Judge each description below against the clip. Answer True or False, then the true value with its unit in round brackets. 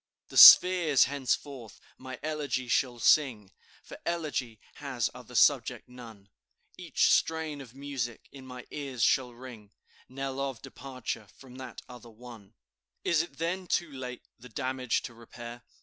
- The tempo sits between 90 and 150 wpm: True (140 wpm)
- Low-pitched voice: True (130 Hz)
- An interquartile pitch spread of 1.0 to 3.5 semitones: True (2.9 semitones)